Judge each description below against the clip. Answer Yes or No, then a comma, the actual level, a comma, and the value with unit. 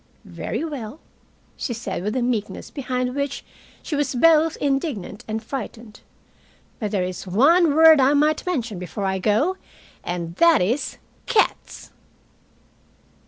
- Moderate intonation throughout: No, wide, 6.3 semitones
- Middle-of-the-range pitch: No, very high, 255 Hz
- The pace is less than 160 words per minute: Yes, slow, 135 wpm